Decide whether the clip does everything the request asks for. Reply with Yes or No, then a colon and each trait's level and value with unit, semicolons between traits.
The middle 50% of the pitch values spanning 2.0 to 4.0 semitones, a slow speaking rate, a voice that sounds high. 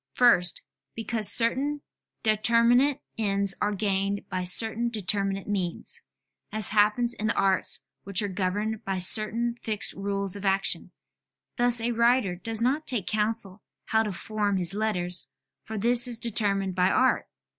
No: average, 3.0 semitones; average, 145 wpm; high, 210 Hz